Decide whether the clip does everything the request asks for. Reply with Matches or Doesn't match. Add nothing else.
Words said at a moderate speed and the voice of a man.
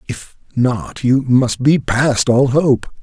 Matches